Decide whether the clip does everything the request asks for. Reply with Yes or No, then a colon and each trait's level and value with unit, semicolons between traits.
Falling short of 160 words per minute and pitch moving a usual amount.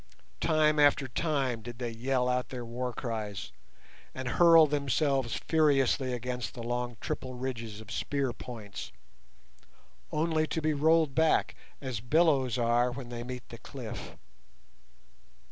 Yes: slow, 135 wpm; average, 3.5 semitones